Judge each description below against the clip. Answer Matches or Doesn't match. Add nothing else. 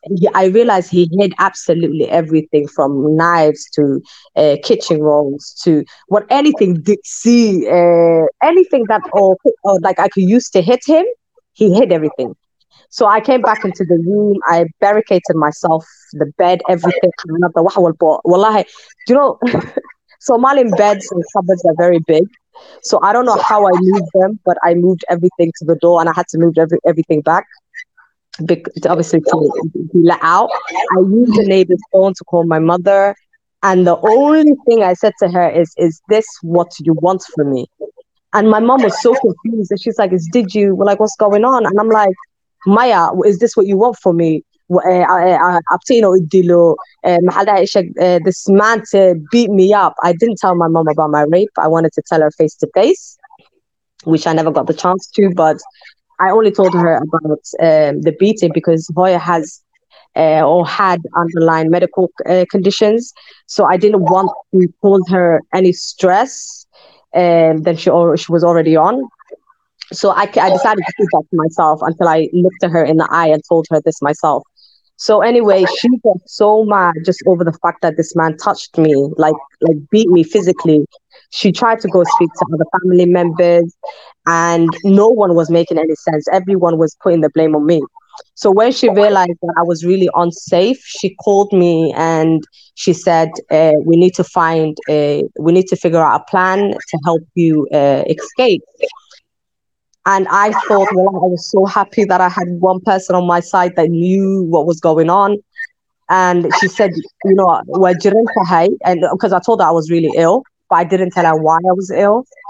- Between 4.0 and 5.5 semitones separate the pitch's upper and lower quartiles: Doesn't match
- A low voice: Doesn't match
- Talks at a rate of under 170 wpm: Doesn't match